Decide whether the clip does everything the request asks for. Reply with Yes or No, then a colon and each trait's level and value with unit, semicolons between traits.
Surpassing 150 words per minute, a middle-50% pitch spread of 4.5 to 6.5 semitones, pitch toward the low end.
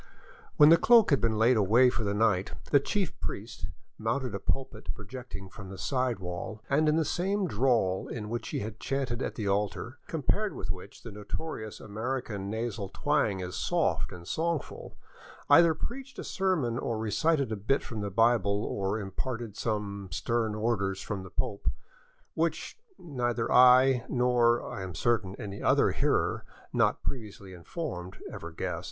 Yes: average, 170 wpm; average, 4.9 semitones; low, 115 Hz